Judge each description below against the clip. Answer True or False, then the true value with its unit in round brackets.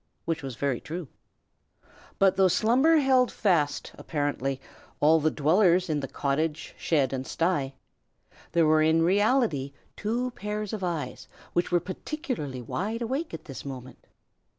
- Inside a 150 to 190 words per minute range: False (140 wpm)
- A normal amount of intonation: False (6.6 semitones)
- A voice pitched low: False (165 Hz)